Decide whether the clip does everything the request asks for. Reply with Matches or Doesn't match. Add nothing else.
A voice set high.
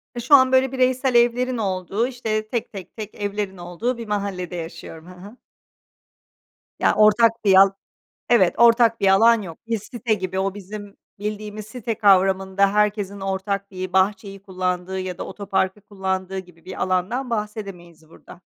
Matches